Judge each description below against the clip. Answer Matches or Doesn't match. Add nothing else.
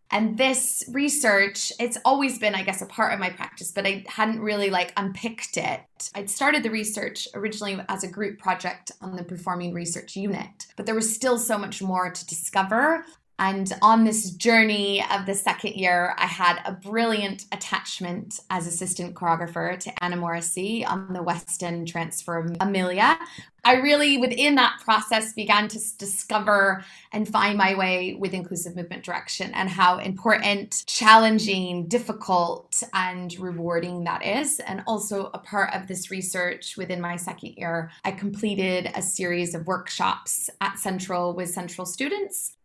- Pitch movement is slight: Doesn't match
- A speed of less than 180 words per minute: Matches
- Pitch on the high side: Matches